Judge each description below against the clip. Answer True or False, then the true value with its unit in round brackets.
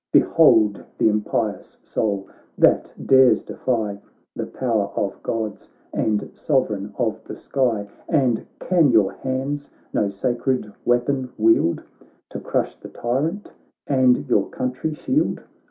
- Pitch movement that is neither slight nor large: True (3.9 semitones)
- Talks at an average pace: False (120 wpm)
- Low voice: True (120 Hz)